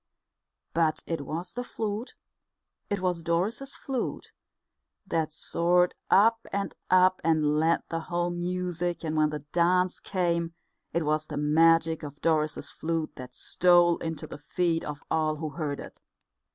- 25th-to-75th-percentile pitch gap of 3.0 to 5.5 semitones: No, narrow, 2.5 semitones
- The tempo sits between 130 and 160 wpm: Yes, average, 150 wpm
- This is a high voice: No, medium, 170 Hz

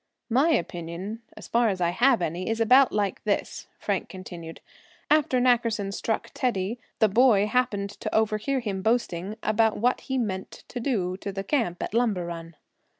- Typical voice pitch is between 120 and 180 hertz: No, high, 215 Hz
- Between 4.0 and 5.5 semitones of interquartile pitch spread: Yes, average, 4.3 semitones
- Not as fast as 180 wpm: Yes, average, 170 wpm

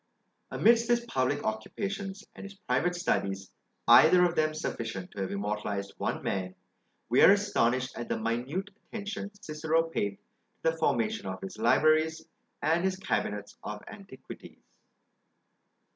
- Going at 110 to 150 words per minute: Yes, average, 140 wpm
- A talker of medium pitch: Yes, medium, 155 Hz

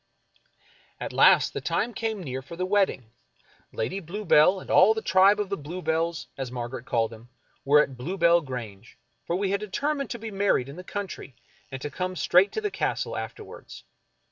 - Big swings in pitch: Yes, wide, 7.1 semitones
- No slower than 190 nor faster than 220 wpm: Yes, average, 195 wpm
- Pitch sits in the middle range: Yes, medium, 180 Hz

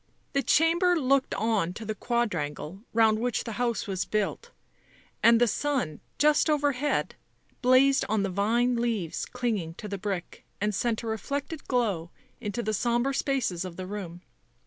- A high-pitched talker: Yes, high, 230 Hz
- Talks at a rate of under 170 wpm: Yes, average, 160 wpm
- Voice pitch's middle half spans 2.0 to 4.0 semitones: No, average, 4.6 semitones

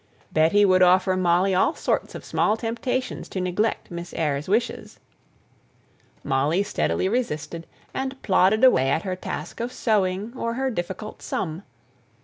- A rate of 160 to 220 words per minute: No, average, 140 wpm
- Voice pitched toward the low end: No, medium, 185 Hz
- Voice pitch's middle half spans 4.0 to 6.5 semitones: Yes, average, 4.6 semitones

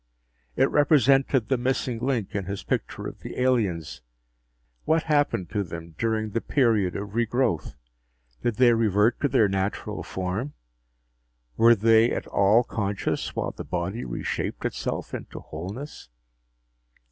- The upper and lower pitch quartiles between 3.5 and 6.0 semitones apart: Yes, average, 4.7 semitones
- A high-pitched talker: No, low, 110 Hz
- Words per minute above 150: No, slow, 135 wpm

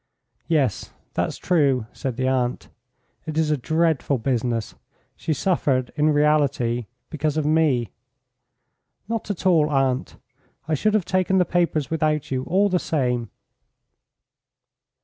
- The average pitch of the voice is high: No, medium, 150 Hz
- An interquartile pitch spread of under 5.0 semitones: Yes, average, 3.9 semitones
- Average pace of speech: No, slow, 130 wpm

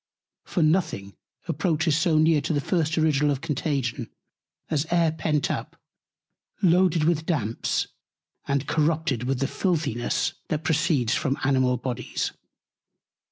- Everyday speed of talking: No, slow, 125 wpm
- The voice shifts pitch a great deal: No, average, 3.1 semitones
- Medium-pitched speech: Yes, medium, 150 Hz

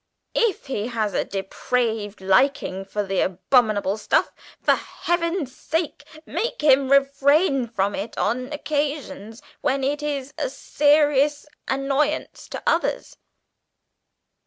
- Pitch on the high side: Yes, very high, 270 Hz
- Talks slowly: Yes, slow, 115 wpm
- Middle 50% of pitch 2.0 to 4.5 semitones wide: No, wide, 5.4 semitones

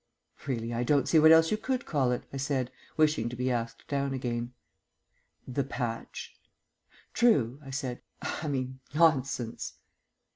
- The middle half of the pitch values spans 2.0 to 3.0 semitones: No, average, 3.5 semitones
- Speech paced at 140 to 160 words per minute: Yes, average, 150 wpm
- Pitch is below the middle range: Yes, low, 130 Hz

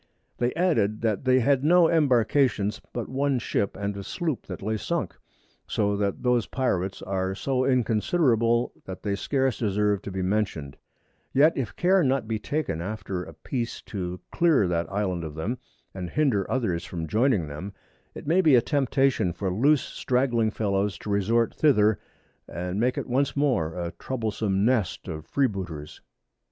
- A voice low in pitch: Yes, low, 110 Hz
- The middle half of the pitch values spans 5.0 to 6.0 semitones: Yes, wide, 5.5 semitones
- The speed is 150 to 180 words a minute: Yes, average, 165 wpm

